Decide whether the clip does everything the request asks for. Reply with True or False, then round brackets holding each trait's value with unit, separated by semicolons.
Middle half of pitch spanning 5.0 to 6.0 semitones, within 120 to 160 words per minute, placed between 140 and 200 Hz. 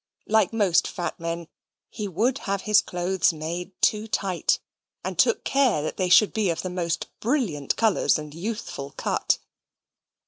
False (4.2 semitones; 150 wpm; 185 Hz)